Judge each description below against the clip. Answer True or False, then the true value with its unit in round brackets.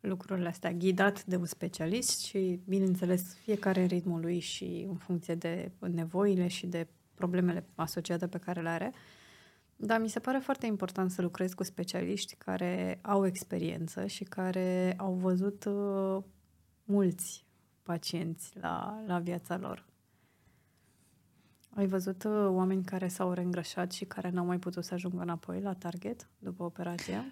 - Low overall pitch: False (185 Hz)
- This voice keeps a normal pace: True (145 wpm)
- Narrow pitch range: True (1.9 semitones)